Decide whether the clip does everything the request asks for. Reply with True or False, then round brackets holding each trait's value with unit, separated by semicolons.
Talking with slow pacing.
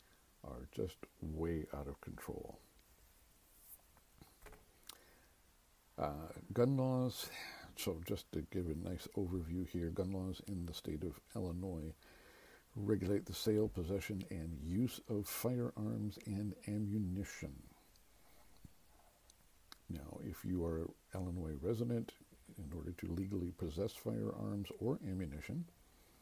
True (110 wpm)